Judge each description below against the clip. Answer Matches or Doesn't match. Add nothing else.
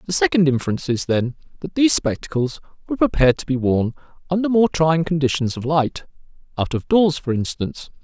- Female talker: Doesn't match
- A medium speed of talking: Matches